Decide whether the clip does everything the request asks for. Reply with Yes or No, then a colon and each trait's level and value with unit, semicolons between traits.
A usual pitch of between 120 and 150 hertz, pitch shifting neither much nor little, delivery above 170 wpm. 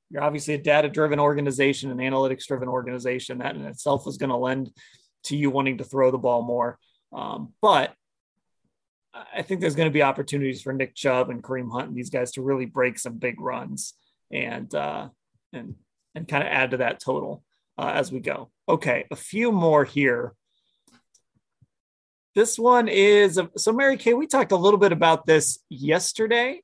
Yes: medium, 140 Hz; average, 4.4 semitones; average, 180 wpm